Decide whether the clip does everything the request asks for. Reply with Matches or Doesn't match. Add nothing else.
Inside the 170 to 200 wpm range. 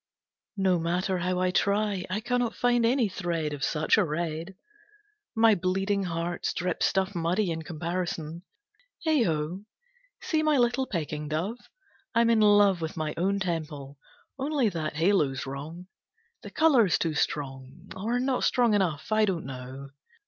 Doesn't match